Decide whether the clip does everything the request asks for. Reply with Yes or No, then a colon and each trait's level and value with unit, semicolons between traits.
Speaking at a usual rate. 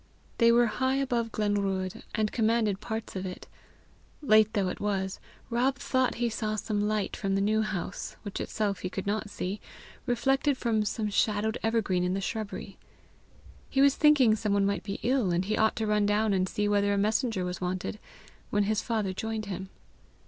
Yes: average, 190 wpm